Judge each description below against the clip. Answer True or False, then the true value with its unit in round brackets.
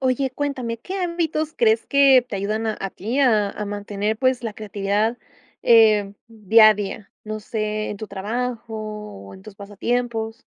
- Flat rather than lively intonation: False (3.1 semitones)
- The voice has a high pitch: True (220 Hz)